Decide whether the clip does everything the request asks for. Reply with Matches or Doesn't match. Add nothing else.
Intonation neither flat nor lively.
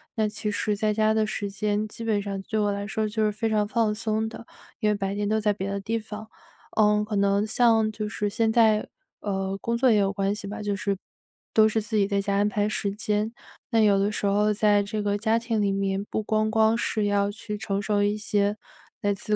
Doesn't match